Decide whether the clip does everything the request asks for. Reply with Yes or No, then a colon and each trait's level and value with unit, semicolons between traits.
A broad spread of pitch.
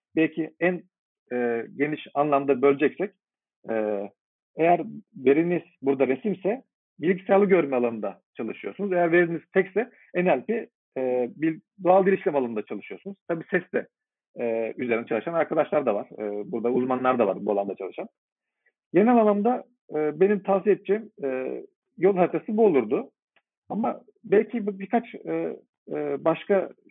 Yes: wide, 7.2 semitones